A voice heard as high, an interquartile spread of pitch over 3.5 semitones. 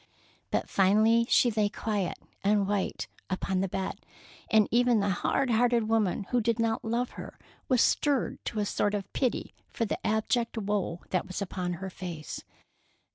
No: high, 210 Hz; average, 3.2 semitones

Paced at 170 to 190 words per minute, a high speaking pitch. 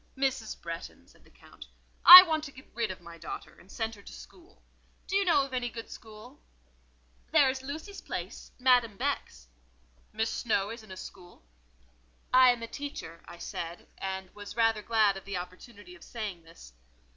Yes: average, 180 wpm; high, 220 Hz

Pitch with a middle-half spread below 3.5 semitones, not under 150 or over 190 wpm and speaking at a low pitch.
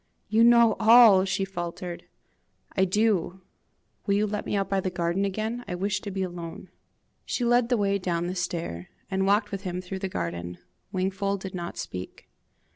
No: average, 2.7 semitones; average, 185 wpm; high, 190 Hz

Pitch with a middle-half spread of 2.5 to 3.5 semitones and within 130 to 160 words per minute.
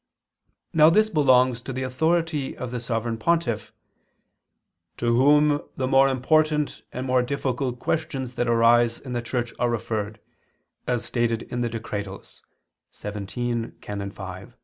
Yes: average, 2.8 semitones; average, 145 wpm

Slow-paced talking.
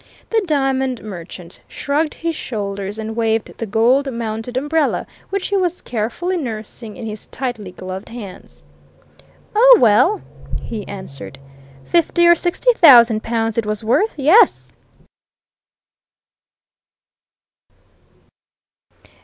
Yes: slow, 110 wpm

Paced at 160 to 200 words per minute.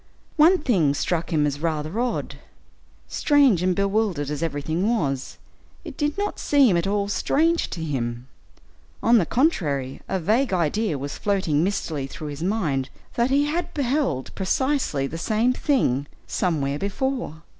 No: average, 150 wpm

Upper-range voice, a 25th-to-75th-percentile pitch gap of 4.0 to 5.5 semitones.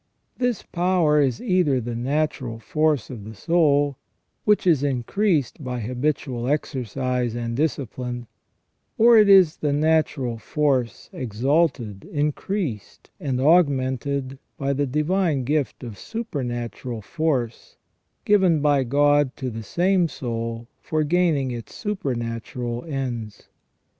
No: medium, 140 Hz; average, 4.5 semitones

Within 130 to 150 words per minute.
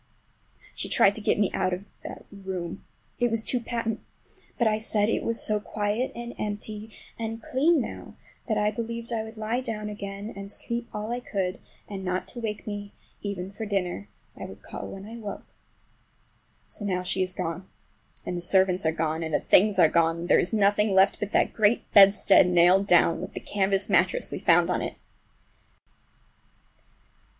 No: average, 185 wpm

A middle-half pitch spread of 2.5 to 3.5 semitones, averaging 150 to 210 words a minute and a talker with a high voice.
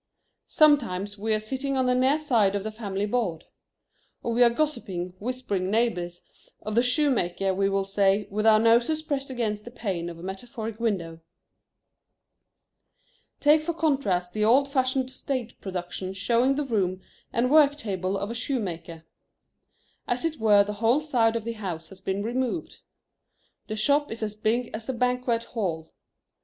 No: average, 4.7 semitones; average, 165 wpm; high, 225 Hz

